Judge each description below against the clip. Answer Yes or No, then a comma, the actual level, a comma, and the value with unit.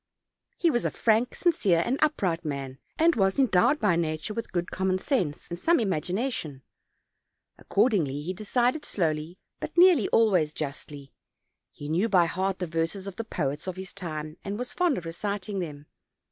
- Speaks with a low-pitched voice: No, medium, 185 Hz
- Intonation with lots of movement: Yes, wide, 6.2 semitones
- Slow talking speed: No, average, 175 wpm